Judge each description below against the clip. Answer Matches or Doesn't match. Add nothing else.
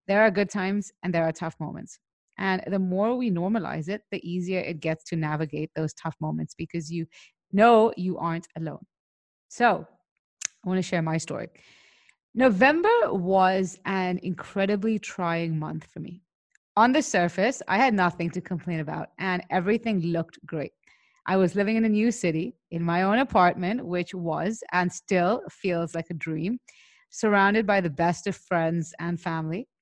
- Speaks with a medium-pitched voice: Matches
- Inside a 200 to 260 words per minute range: Doesn't match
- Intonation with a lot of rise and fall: Doesn't match